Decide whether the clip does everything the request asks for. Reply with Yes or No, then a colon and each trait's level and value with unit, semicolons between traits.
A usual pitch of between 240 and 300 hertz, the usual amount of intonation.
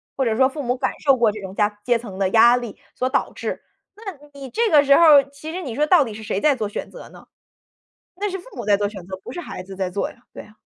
No: high, 245 Hz; wide, 6.0 semitones